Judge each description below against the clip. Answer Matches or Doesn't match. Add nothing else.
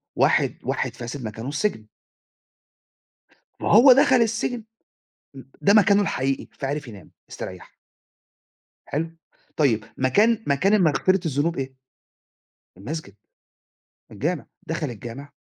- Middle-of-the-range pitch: Matches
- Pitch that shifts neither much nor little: Doesn't match